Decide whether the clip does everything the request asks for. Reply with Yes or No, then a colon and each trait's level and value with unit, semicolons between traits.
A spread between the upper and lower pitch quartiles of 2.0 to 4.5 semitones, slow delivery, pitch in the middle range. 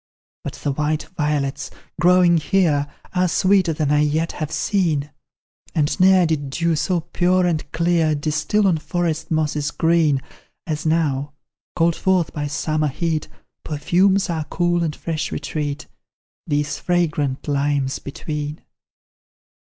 Yes: average, 2.8 semitones; slow, 130 wpm; medium, 155 Hz